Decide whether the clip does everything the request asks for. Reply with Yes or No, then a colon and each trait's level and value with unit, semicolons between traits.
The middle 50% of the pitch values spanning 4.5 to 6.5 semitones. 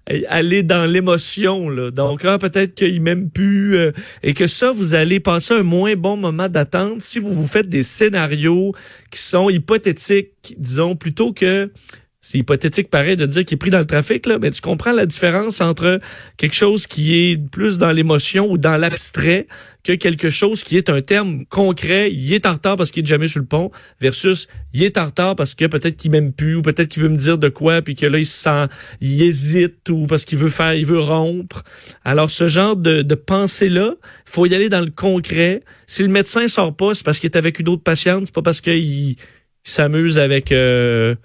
No: average, 3.8 semitones